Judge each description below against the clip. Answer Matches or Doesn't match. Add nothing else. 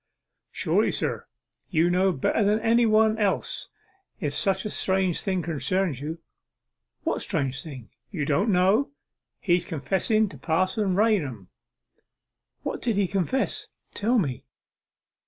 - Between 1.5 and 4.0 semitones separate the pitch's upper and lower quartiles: Doesn't match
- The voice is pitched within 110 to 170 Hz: Doesn't match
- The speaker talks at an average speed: Doesn't match